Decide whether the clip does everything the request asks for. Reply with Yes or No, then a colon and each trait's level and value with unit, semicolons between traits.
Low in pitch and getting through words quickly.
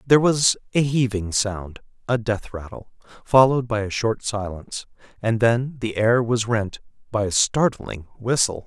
No: low, 115 Hz; average, 160 wpm